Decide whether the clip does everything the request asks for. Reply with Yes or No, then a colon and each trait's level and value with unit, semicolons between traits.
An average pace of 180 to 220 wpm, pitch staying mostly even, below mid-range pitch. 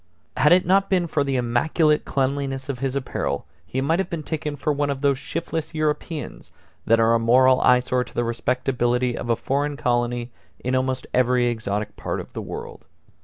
No: average, 190 wpm; average, 3.4 semitones; low, 130 Hz